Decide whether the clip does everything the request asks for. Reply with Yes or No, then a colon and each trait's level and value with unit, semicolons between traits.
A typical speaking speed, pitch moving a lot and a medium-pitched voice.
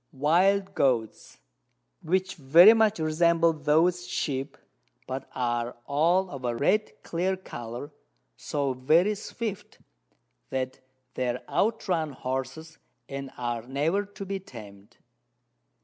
No: slow, 115 wpm; wide, 6.2 semitones; medium, 155 Hz